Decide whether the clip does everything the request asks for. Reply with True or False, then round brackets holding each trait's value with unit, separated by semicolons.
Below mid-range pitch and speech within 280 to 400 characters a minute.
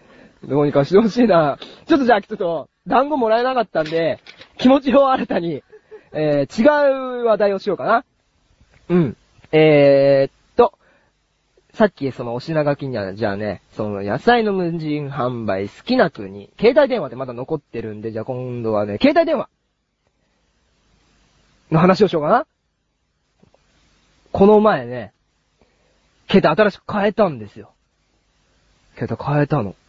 False (155 Hz; 285 characters per minute)